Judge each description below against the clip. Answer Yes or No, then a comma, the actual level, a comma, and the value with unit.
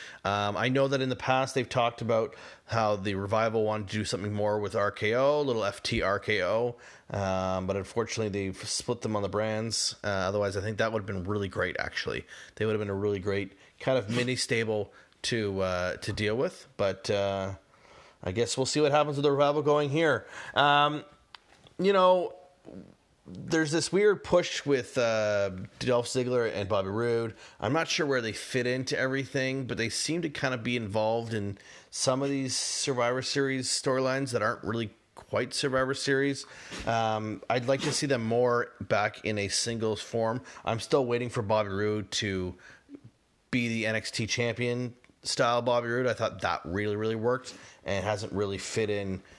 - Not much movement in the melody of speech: No, average, 4.0 semitones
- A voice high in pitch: No, low, 115 Hz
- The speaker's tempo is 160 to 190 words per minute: Yes, average, 185 wpm